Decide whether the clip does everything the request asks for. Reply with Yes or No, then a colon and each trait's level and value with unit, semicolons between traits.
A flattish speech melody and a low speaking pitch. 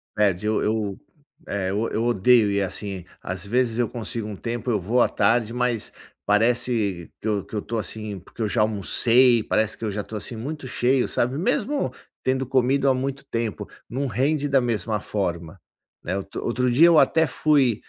No: average, 3.5 semitones; low, 115 Hz